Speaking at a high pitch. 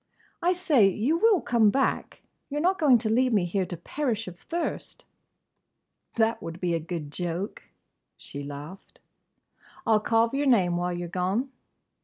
Yes: high, 215 Hz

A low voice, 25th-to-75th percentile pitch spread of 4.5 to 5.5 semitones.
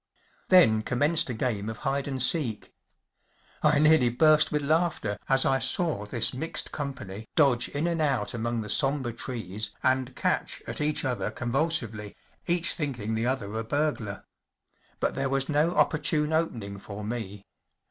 Yes: low, 130 Hz; average, 5.2 semitones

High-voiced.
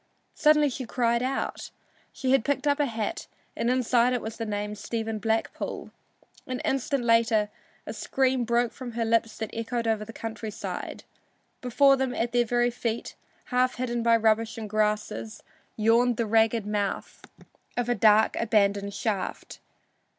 Yes: high, 230 Hz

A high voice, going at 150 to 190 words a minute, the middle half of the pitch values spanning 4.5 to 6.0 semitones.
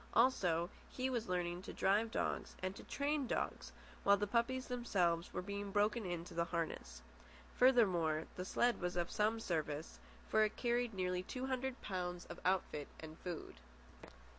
Yes: high, 195 Hz; average, 165 wpm; average, 5.3 semitones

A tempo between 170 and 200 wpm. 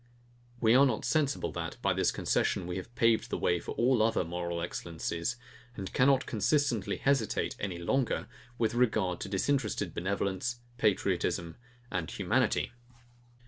No: average, 145 wpm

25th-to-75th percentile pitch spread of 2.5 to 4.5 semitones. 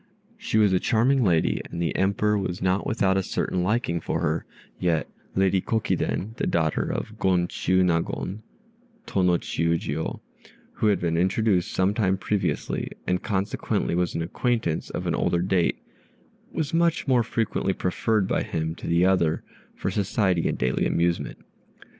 Yes: average, 3.6 semitones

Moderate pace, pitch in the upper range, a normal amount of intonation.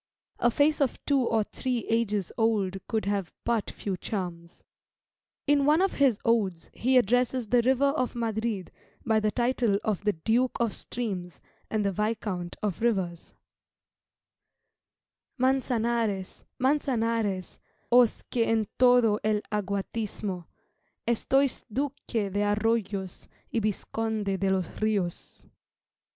No: slow, 125 wpm; high, 220 Hz; average, 3.6 semitones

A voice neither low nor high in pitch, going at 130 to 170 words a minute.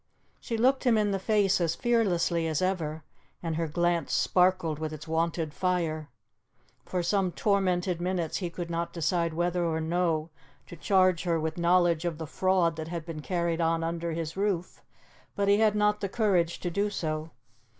No: medium, 175 Hz; average, 180 wpm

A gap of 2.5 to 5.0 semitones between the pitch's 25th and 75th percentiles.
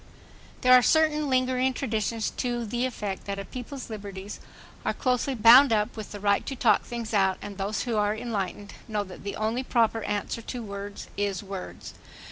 Yes: average, 3.6 semitones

